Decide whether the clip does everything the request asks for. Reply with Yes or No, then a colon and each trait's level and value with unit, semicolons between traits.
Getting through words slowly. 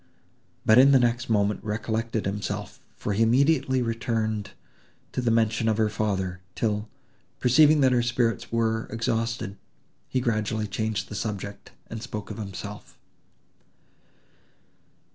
Yes: slow, 130 wpm